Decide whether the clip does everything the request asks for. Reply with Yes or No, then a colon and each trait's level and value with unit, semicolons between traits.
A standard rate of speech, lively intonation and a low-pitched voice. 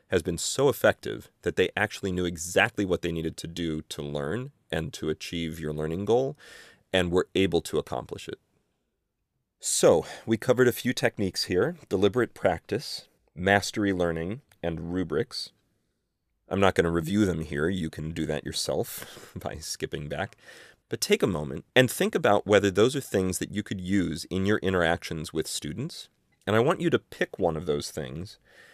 No: average, 180 wpm; average, 4.1 semitones; very low, 90 Hz